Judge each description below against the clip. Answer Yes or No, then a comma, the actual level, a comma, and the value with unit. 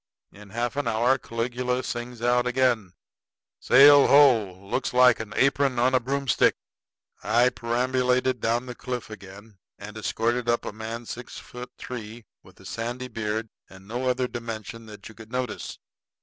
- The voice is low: Yes, low, 120 Hz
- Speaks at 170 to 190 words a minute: No, average, 160 wpm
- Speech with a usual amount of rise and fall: No, narrow, 2.3 semitones